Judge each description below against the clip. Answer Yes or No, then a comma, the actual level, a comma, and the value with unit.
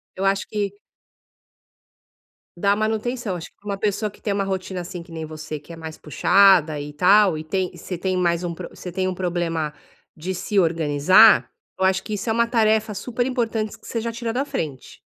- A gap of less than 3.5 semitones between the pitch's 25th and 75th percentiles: No, average, 4.2 semitones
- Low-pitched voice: No, high, 190 Hz